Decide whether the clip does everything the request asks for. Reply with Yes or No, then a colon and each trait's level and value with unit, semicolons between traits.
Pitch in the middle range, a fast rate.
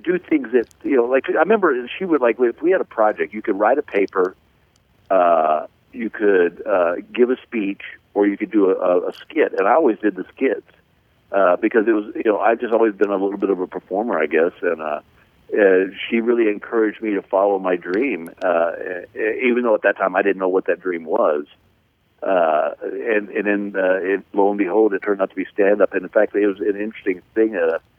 No: low, 105 Hz; fast, 230 wpm